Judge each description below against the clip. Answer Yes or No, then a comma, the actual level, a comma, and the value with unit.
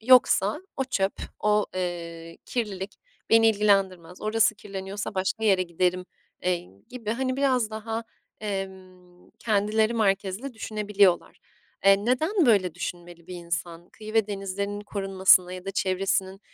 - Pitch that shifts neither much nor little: Yes, average, 3.1 semitones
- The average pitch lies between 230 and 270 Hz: No, high, 200 Hz